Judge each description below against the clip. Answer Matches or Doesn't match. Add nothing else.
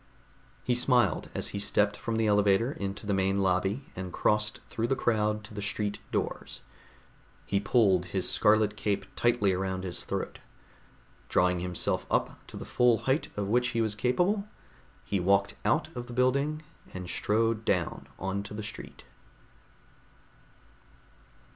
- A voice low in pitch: Matches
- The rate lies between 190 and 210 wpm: Doesn't match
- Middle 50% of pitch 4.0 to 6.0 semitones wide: Doesn't match